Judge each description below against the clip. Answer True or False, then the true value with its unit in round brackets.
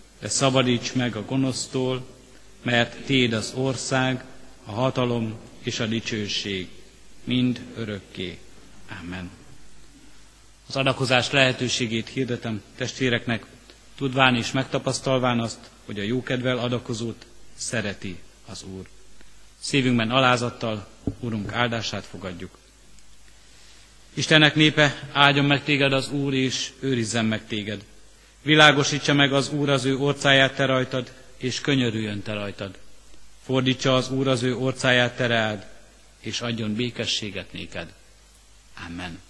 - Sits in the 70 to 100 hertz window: False (120 Hz)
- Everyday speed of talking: True (115 wpm)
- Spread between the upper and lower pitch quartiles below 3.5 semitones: False (3.8 semitones)